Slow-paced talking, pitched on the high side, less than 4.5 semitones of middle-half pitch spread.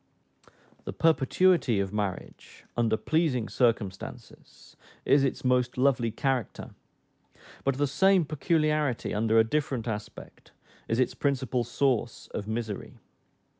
No: slow, 115 wpm; low, 125 Hz; average, 4.1 semitones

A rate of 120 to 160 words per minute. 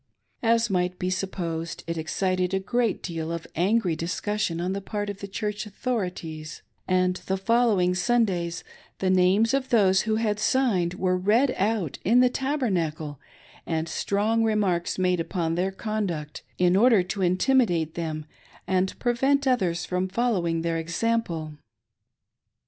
Yes: average, 145 wpm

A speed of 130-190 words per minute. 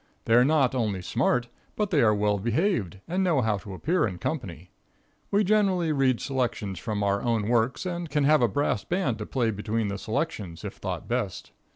No: average, 200 wpm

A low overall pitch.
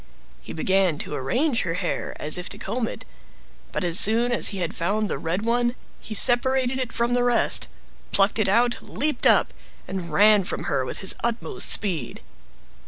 No: high, 210 Hz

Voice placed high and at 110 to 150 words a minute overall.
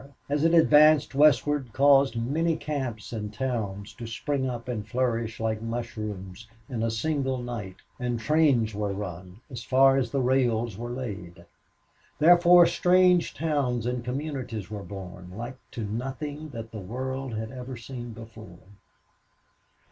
No: low, 120 Hz; average, 145 wpm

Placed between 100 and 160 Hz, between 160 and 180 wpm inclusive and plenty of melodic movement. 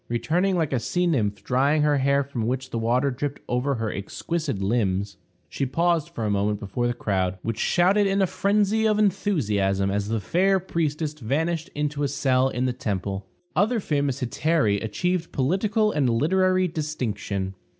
Yes: medium, 140 Hz; average, 170 wpm; wide, 7.5 semitones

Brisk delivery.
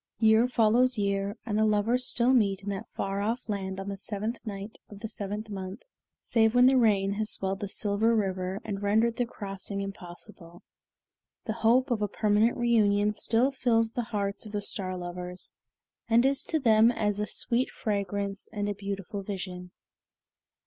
No: average, 175 wpm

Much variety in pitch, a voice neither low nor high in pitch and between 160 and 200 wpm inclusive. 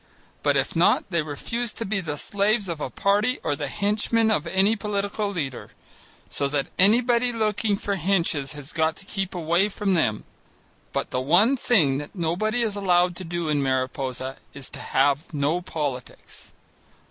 Yes: wide, 6.1 semitones; medium, 180 Hz; average, 170 wpm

